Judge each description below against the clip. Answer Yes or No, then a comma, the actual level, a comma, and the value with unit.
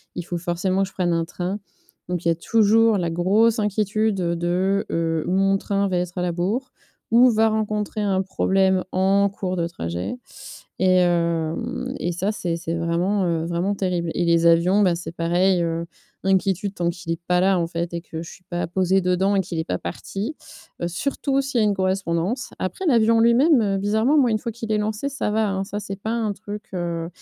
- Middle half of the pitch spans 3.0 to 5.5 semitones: Yes, average, 3.5 semitones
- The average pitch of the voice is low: No, high, 190 Hz